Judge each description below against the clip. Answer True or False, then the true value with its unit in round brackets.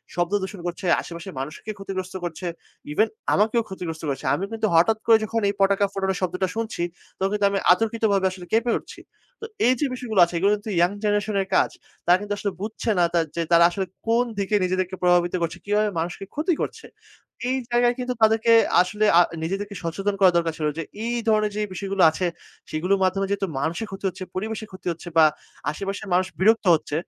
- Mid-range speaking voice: False (195 Hz)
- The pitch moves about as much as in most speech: True (3.3 semitones)